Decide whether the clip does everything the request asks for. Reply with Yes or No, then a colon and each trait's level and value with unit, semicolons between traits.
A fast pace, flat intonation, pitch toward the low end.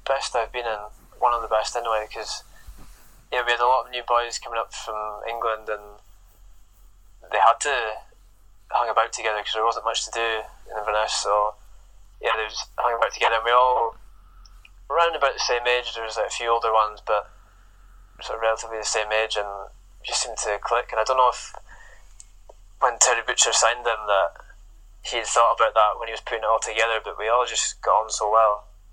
Yes: fast, 215 wpm; narrow, 2.1 semitones; low, 110 Hz